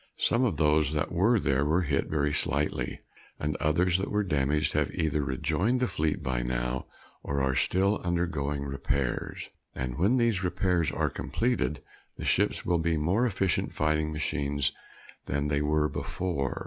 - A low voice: Yes, very low, 75 Hz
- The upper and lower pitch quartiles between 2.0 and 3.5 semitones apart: No, average, 4.3 semitones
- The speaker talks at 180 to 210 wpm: No, average, 160 wpm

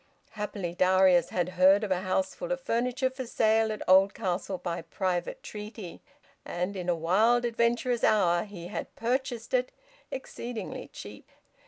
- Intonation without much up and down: No, average, 4.6 semitones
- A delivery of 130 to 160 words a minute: Yes, average, 145 wpm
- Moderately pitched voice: No, high, 210 Hz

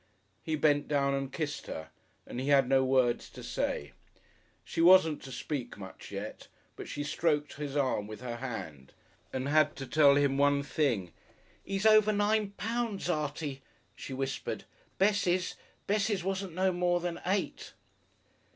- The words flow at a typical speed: Yes, average, 155 wpm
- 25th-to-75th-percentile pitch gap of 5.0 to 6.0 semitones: Yes, wide, 5.5 semitones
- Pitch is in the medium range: Yes, medium, 145 Hz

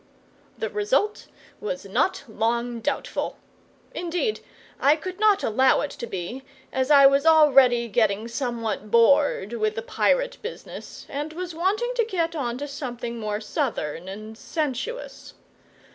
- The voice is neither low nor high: No, very high, 270 Hz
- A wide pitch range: Yes, wide, 6.7 semitones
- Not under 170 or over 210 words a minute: No, average, 140 wpm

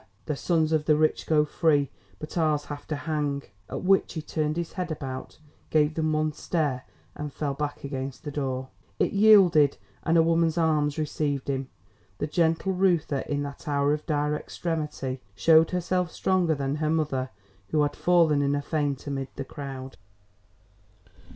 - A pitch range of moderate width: No, narrow, 2.3 semitones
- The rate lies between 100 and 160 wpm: No, average, 170 wpm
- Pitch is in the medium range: Yes, medium, 150 Hz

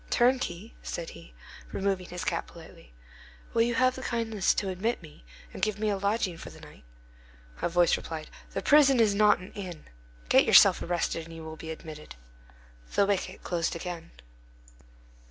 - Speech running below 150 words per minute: No, average, 175 wpm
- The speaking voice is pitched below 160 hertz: No, medium, 185 Hz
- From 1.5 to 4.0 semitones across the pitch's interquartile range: No, average, 4.7 semitones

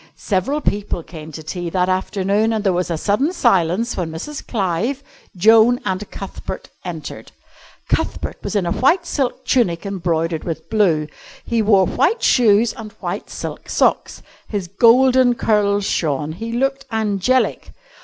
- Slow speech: No, average, 150 wpm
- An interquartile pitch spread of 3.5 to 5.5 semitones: Yes, average, 5.1 semitones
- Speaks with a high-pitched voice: Yes, high, 205 Hz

